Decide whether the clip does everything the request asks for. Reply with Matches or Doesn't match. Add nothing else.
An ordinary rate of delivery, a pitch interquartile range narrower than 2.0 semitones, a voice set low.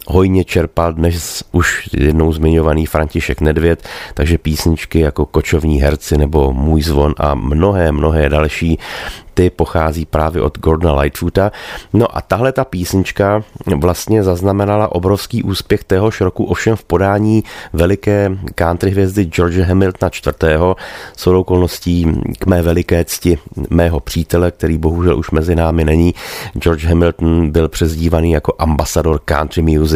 Doesn't match